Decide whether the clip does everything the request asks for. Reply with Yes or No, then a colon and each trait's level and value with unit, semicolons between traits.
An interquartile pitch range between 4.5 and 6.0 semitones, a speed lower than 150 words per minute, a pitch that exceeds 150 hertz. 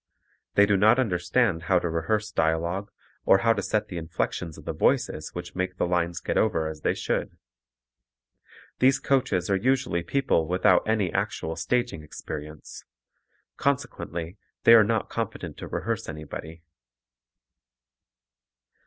No: average, 4.8 semitones; average, 140 wpm; very low, 90 Hz